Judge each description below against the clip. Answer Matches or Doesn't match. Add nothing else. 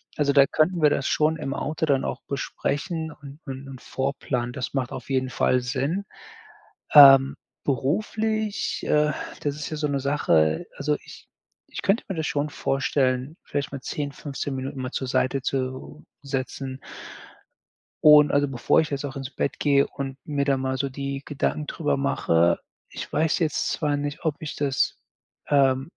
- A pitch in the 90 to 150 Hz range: Matches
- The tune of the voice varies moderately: Doesn't match